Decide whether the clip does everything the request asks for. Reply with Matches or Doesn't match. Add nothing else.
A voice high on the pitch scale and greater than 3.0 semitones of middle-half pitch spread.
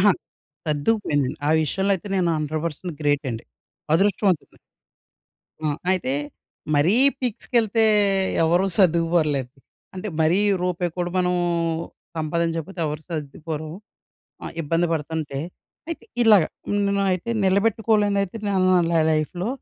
Doesn't match